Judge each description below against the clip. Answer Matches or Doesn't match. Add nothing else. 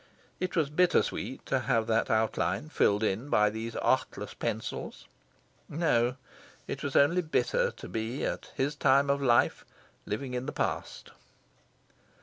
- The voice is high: Doesn't match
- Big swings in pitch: Doesn't match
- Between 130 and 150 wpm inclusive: Matches